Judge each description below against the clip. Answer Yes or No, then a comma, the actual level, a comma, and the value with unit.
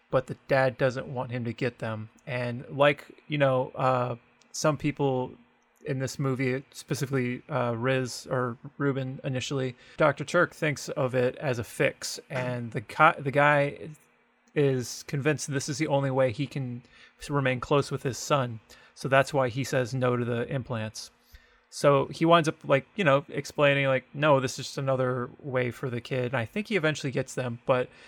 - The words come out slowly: No, average, 190 wpm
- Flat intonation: Yes, narrow, 2.3 semitones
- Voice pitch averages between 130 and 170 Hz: Yes, low, 135 Hz